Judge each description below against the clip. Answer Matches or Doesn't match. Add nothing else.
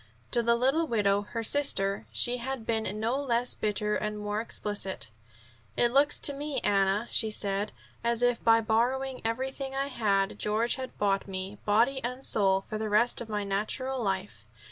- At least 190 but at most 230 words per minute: Doesn't match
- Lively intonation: Doesn't match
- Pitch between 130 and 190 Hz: Doesn't match